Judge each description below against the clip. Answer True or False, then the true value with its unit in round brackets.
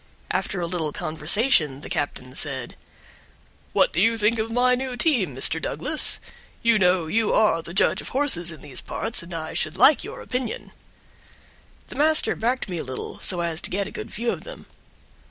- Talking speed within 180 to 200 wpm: True (190 wpm)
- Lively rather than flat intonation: True (7.5 semitones)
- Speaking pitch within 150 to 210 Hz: True (190 Hz)